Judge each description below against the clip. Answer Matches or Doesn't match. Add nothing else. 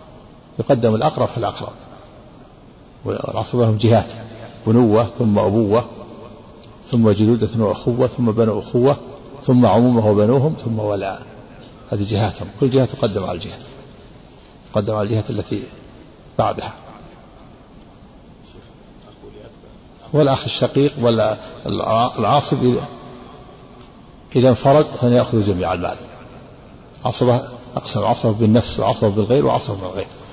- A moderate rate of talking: Matches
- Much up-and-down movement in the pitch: Doesn't match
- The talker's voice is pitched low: Matches